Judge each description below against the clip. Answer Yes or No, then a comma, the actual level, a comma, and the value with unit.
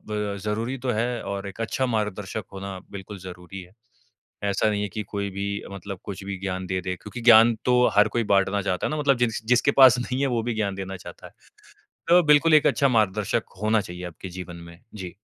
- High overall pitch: No, low, 105 Hz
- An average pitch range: Yes, average, 3.7 semitones